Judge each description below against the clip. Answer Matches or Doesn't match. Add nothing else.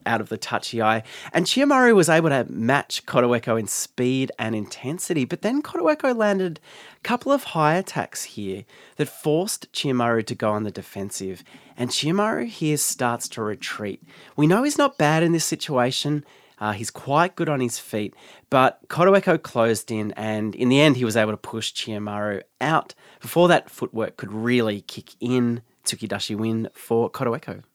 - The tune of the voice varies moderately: Doesn't match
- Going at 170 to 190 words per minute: Matches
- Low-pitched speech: Matches